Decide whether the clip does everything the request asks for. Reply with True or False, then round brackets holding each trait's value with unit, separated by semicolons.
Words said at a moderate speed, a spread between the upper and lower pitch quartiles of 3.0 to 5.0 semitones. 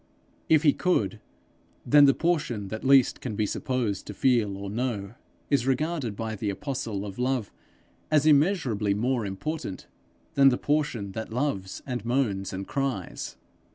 False (155 wpm; 5.4 semitones)